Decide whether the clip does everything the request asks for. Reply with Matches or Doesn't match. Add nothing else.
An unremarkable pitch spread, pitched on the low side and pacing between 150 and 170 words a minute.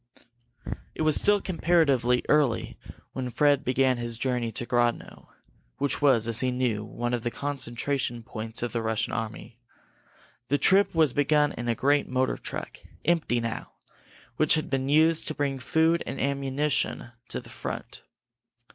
Matches